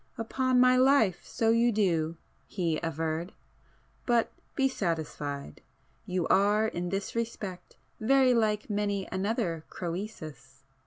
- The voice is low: No, high, 200 Hz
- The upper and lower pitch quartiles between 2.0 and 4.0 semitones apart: No, wide, 5.5 semitones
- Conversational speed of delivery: No, slow, 105 wpm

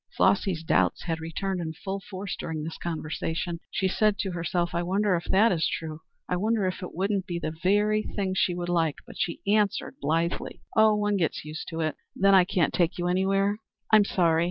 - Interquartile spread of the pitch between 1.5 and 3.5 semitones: Yes, average, 3.1 semitones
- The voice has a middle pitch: Yes, medium, 180 Hz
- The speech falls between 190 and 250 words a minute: Yes, fast, 205 wpm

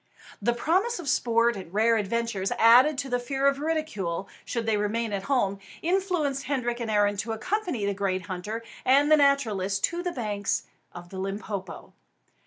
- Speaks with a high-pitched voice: Yes, high, 230 Hz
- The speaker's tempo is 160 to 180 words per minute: Yes, average, 175 wpm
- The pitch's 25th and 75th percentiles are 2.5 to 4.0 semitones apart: No, wide, 5.6 semitones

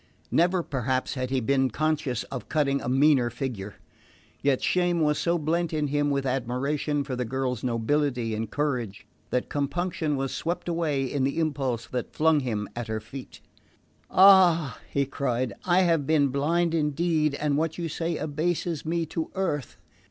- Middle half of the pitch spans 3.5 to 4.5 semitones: Yes, average, 3.9 semitones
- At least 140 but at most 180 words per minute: Yes, average, 165 wpm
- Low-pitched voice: No, medium, 145 Hz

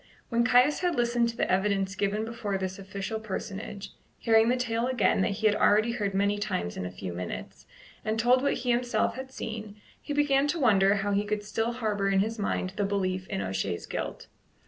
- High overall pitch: Yes, high, 210 Hz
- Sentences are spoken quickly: Yes, fast, 210 wpm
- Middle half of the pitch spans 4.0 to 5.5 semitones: No, average, 3.4 semitones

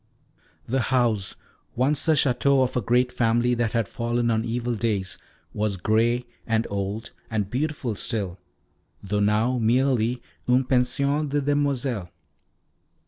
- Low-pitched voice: Yes, low, 120 Hz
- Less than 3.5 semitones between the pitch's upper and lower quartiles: Yes, average, 2.7 semitones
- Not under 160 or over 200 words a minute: No, slow, 135 wpm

